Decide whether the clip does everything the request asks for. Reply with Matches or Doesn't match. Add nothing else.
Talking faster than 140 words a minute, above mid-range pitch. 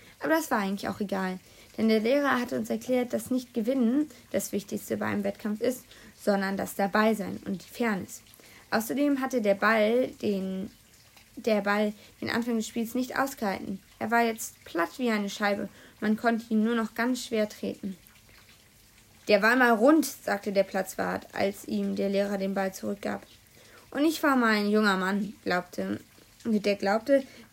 Matches